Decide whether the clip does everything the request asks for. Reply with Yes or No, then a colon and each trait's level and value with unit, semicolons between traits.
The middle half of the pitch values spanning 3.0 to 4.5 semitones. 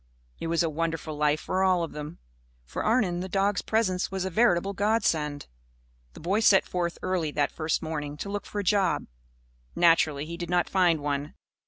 Yes: average, 3.6 semitones